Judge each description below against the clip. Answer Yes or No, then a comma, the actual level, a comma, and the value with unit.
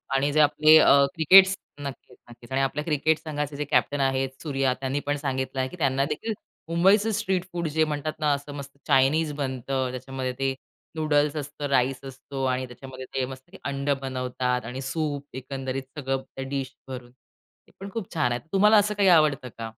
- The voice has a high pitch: No, medium, 140 Hz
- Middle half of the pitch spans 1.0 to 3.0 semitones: Yes, average, 2.7 semitones